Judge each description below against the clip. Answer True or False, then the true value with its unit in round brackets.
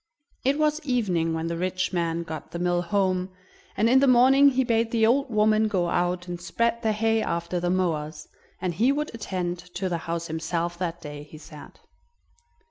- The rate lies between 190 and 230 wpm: True (195 wpm)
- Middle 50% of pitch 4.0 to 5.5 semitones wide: True (5.1 semitones)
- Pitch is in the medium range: True (180 Hz)